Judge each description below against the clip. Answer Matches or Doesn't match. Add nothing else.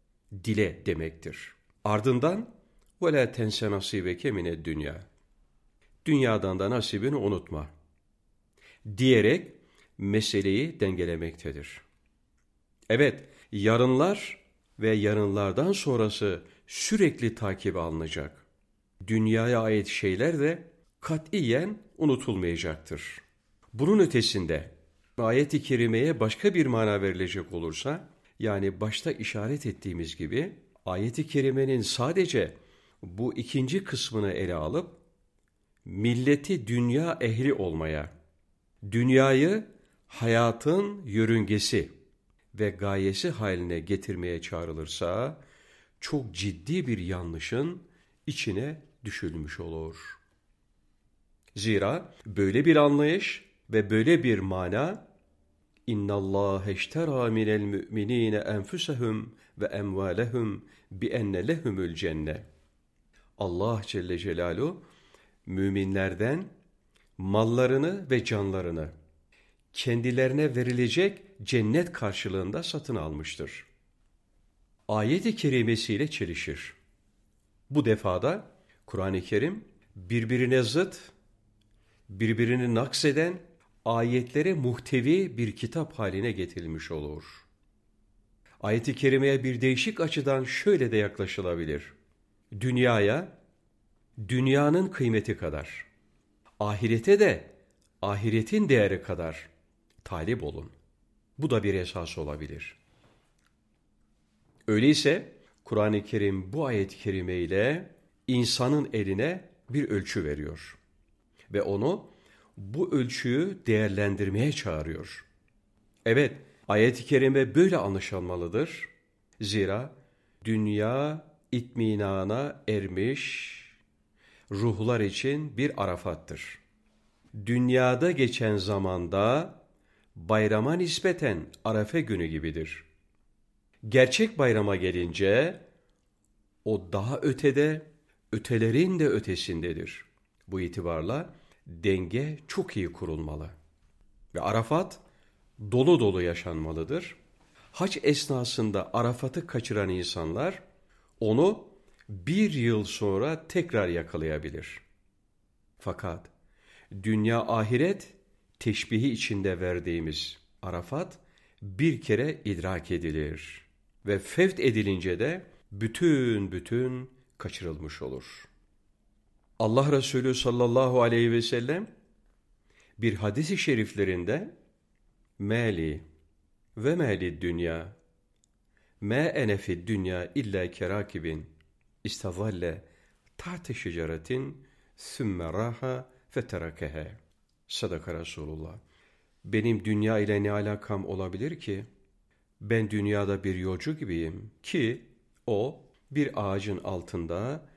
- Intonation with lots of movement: Matches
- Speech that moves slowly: Matches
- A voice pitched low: Matches